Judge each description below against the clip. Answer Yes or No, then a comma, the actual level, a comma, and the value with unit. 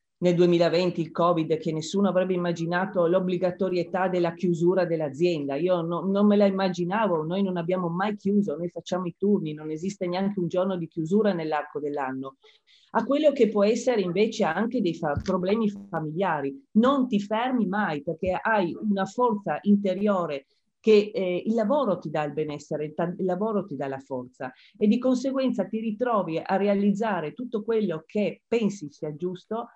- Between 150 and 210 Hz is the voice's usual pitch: Yes, medium, 185 Hz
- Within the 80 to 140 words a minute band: No, fast, 170 wpm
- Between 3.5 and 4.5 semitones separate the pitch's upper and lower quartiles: Yes, average, 3.9 semitones